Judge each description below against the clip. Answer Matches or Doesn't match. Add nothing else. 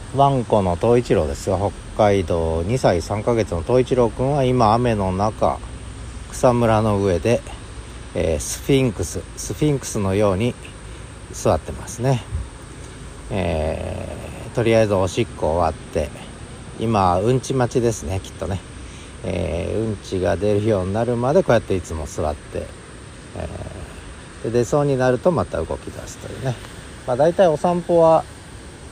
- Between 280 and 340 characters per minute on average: Matches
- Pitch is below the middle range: Matches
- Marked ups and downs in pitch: Doesn't match